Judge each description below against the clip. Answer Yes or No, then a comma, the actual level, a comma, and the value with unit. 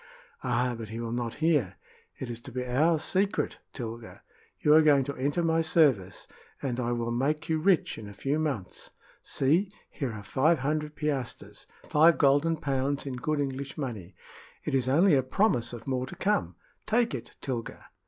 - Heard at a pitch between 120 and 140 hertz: Yes, low, 135 Hz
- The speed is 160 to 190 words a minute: Yes, average, 185 wpm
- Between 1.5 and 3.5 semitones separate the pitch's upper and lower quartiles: No, average, 4.3 semitones